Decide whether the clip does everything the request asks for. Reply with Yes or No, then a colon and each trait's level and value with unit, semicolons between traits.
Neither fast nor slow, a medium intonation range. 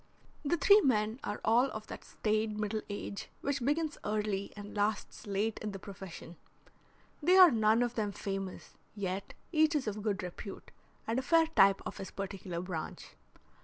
Yes: average, 170 wpm; average, 4.1 semitones